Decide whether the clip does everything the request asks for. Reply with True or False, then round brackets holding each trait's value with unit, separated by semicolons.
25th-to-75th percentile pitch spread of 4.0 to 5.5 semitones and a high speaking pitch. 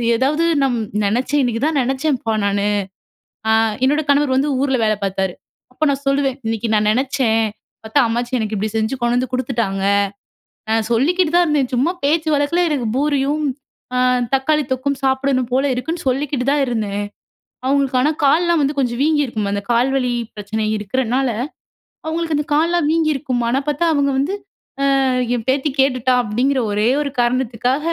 False (3.6 semitones; 265 Hz)